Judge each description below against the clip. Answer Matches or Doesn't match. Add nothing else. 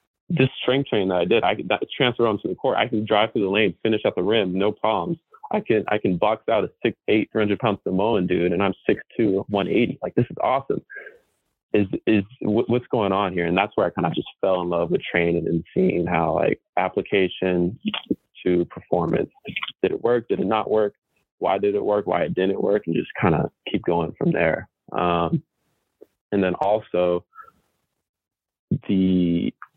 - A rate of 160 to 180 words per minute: Doesn't match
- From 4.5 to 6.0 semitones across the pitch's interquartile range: Matches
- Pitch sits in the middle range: Doesn't match